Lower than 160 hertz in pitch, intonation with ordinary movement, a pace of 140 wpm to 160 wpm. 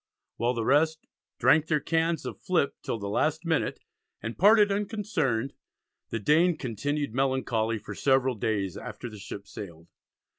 No: low, 135 Hz; wide, 6.4 semitones; average, 150 wpm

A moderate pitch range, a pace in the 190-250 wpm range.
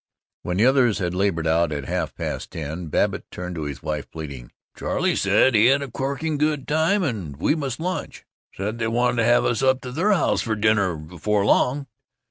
No: wide, 7.8 semitones; average, 200 wpm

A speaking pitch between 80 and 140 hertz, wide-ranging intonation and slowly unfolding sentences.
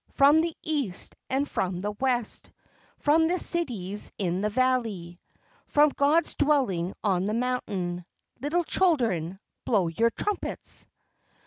No: high, 240 Hz; wide, 7.5 semitones; slow, 125 wpm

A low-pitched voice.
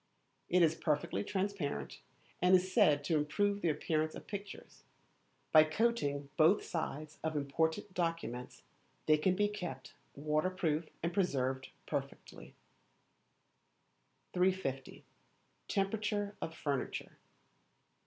No: medium, 165 Hz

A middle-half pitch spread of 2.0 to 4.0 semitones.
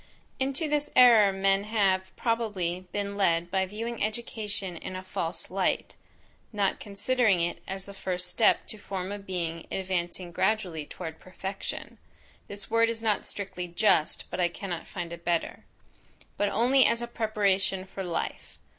Yes: average, 3.1 semitones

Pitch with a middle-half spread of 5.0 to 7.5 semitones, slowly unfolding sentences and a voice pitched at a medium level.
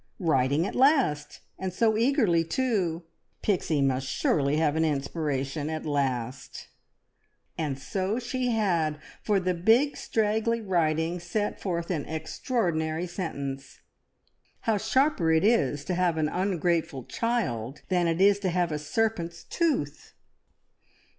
Yes: wide, 5.6 semitones; slow, 130 wpm; medium, 170 Hz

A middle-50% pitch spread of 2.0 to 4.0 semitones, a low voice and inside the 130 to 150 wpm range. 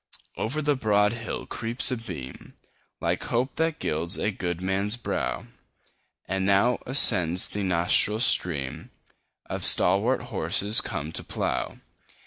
No: average, 5.0 semitones; low, 105 Hz; slow, 135 wpm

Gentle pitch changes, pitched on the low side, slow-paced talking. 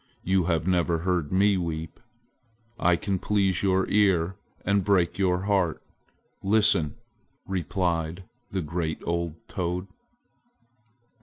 Yes: narrow, 2.3 semitones; very low, 90 Hz; slow, 110 wpm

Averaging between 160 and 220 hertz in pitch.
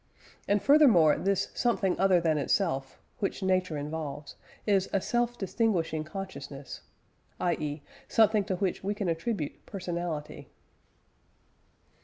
Yes: medium, 185 Hz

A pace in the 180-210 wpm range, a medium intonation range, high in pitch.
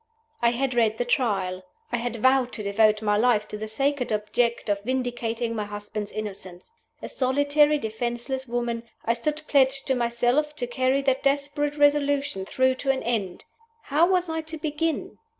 No: average, 170 wpm; average, 4.3 semitones; high, 245 Hz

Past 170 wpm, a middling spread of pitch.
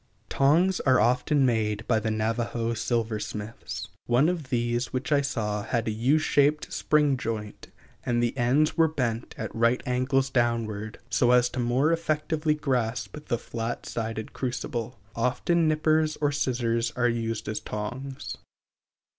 No: average, 145 wpm; average, 3.8 semitones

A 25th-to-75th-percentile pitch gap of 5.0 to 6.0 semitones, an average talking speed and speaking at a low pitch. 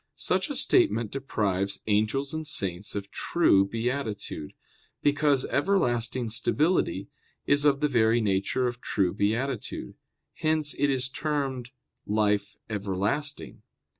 No: wide, 5.6 semitones; slow, 115 wpm; low, 120 Hz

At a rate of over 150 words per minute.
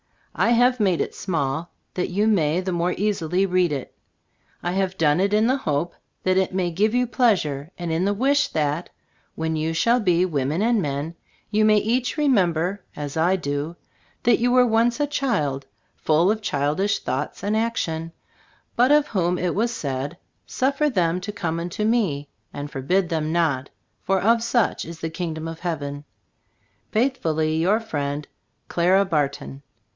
Yes: average, 175 wpm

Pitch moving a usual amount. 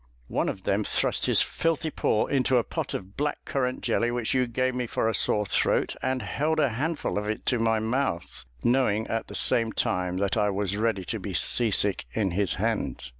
Yes: average, 4.0 semitones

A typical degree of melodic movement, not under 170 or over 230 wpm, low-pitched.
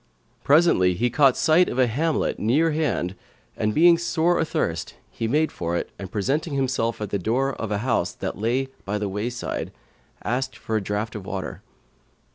No: wide, 6.3 semitones; average, 180 wpm; low, 120 Hz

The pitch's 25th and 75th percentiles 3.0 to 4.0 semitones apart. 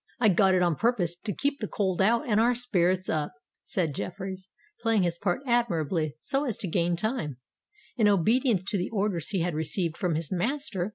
No: average, 4.7 semitones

